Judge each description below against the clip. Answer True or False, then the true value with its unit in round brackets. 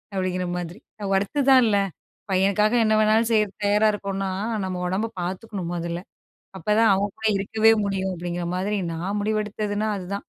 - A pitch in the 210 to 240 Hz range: False (200 Hz)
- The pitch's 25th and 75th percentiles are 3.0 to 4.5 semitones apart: False (2.5 semitones)